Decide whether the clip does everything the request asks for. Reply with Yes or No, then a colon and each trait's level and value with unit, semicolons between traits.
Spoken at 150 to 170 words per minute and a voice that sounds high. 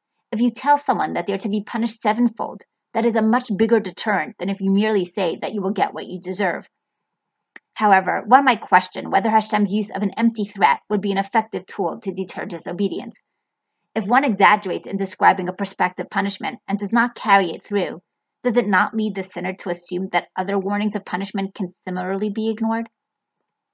No: average, 200 wpm; high, 205 Hz